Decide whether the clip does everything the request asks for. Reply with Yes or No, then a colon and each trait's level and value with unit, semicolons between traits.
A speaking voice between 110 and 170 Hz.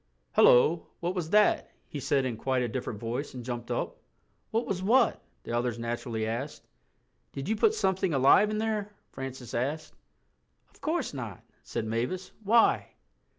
Yes: low, 135 Hz